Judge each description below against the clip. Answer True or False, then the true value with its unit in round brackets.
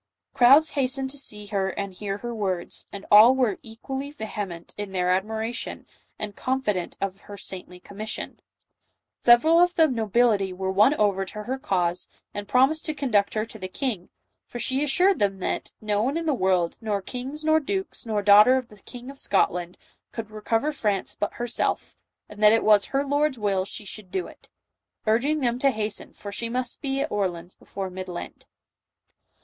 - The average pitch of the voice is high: True (215 Hz)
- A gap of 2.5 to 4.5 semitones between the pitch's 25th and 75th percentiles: False (5.0 semitones)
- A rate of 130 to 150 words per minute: False (190 wpm)